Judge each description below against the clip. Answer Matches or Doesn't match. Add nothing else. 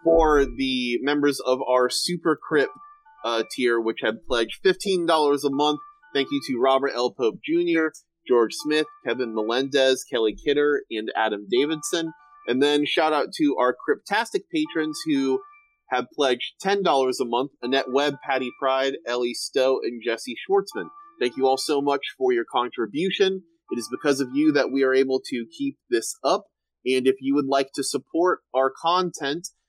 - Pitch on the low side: Doesn't match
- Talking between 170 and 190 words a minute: Matches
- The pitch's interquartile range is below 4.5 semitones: Doesn't match